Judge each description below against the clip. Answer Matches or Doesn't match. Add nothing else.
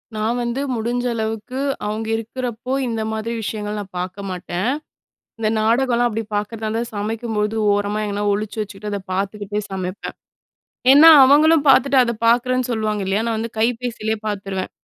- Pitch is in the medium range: Doesn't match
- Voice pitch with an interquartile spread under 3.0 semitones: Matches